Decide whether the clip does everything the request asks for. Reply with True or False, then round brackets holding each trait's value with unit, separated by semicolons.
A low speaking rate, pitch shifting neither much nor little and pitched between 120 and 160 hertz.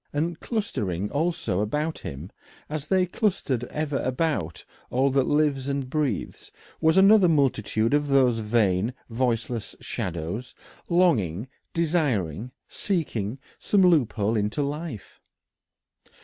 False (110 wpm; 6.7 semitones; 135 Hz)